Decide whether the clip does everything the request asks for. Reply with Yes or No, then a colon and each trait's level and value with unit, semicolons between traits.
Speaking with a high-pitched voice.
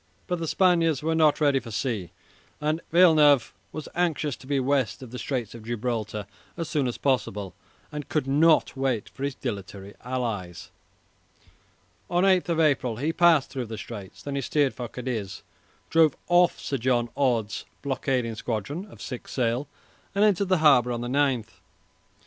No: low, 135 Hz